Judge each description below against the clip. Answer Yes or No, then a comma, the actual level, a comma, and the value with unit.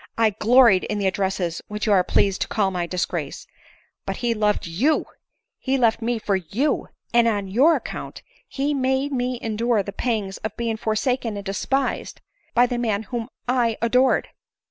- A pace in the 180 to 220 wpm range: Yes, average, 185 wpm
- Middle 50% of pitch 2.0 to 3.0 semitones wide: No, average, 3.7 semitones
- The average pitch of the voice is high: Yes, high, 225 Hz